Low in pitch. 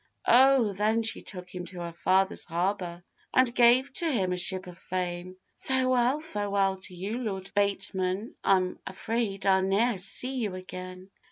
No: high, 195 Hz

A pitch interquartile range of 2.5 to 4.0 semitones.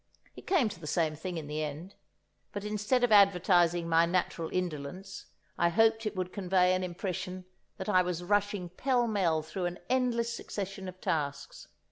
Yes: average, 3.3 semitones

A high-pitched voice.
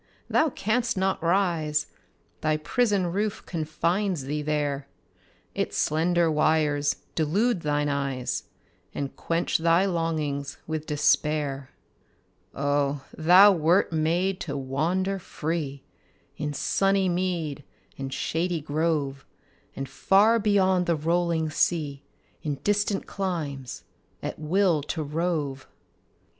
No: medium, 160 Hz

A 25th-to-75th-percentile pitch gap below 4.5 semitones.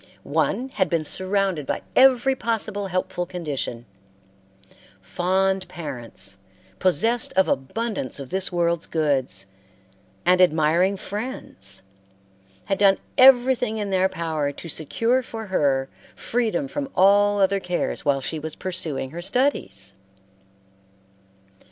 No: wide, 5.6 semitones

